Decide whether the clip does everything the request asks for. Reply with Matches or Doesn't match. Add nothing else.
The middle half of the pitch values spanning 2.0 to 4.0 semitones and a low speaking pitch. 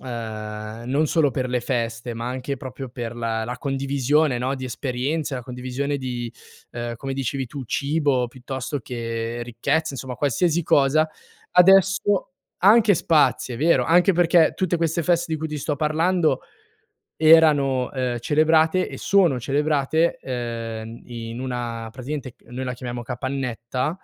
Doesn't match